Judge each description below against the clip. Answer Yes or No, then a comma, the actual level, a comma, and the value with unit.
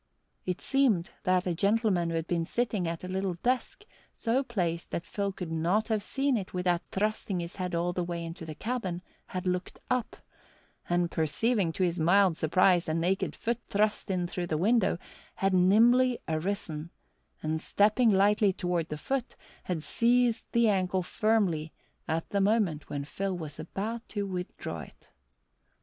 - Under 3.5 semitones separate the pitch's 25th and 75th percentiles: No, average, 4.1 semitones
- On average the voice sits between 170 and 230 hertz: Yes, medium, 185 Hz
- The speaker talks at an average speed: Yes, average, 170 wpm